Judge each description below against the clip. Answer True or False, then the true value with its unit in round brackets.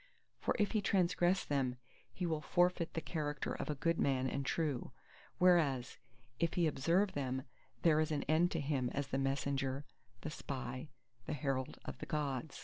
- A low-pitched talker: False (150 Hz)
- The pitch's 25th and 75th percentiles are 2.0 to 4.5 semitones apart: True (3.8 semitones)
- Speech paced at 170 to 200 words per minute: True (175 wpm)